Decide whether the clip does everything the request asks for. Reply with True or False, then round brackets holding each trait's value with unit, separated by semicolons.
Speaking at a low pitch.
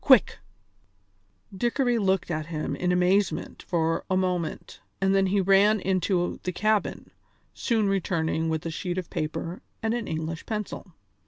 False (185 Hz)